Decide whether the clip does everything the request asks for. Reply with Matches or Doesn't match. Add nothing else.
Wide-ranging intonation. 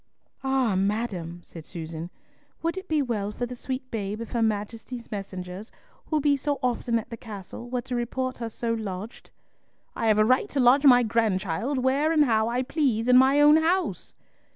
Doesn't match